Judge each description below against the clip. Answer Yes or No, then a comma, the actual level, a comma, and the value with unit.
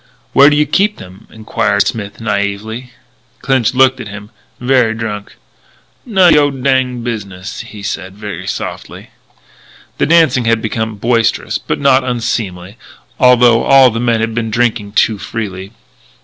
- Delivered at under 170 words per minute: Yes, average, 150 wpm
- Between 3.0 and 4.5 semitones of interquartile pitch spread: Yes, average, 3.8 semitones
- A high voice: No, low, 115 Hz